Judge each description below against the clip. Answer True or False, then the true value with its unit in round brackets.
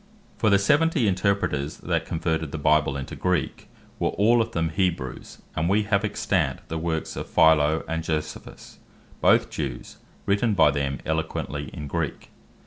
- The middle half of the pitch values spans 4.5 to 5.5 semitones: True (4.8 semitones)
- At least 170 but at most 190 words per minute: False (155 wpm)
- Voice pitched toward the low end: True (80 Hz)